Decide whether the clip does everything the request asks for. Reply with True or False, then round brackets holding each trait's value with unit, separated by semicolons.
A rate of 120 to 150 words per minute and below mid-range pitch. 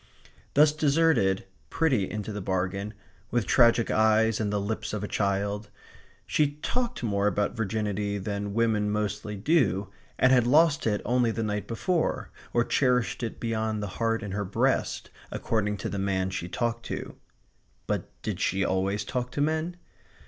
False (165 wpm; 110 Hz)